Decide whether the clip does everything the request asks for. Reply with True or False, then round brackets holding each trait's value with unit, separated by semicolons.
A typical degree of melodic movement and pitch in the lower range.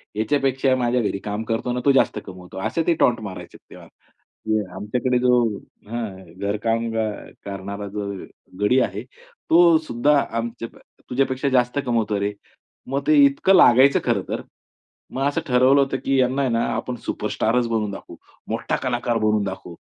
True (4.1 semitones; 120 Hz)